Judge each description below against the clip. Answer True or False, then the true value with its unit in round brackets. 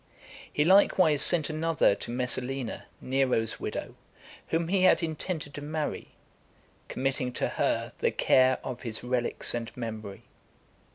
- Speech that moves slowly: True (130 wpm)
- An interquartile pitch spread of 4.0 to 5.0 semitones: True (4.3 semitones)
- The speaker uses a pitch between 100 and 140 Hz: True (135 Hz)